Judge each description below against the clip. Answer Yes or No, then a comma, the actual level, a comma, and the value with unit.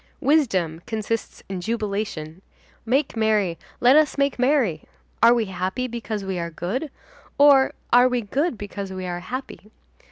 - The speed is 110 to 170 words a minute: Yes, average, 150 wpm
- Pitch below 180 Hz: No, high, 220 Hz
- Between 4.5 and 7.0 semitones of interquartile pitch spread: Yes, average, 5.2 semitones